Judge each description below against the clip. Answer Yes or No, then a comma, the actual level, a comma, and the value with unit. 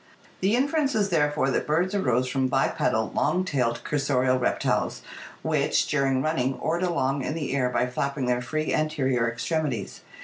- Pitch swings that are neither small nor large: Yes, average, 3.9 semitones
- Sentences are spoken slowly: No, average, 160 wpm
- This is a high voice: No, medium, 140 Hz